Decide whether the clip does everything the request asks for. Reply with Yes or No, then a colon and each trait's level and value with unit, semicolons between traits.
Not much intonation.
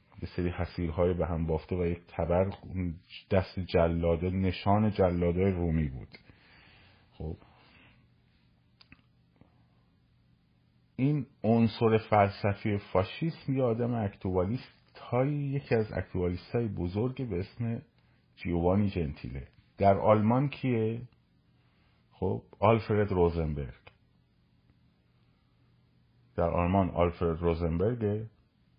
No: average, 4.7 semitones